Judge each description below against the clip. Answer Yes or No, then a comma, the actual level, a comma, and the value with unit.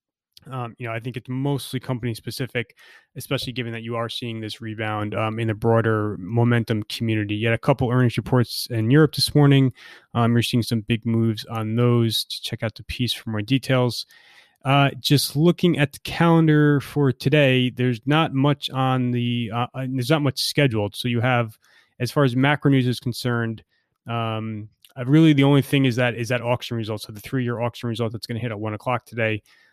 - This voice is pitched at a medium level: No, low, 120 Hz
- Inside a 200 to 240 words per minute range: Yes, fast, 205 wpm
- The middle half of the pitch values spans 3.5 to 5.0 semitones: No, average, 2.7 semitones